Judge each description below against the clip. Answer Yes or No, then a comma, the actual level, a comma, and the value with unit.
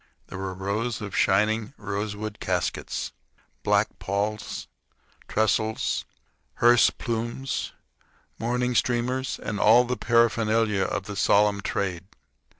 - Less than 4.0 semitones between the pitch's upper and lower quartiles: Yes, narrow, 2.6 semitones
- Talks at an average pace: No, slow, 105 wpm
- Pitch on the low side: Yes, low, 110 Hz